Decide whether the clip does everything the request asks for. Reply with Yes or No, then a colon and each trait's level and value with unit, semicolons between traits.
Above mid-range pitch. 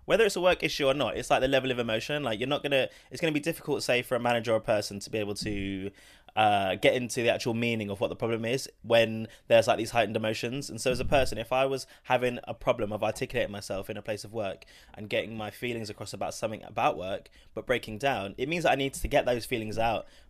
No: low, 120 Hz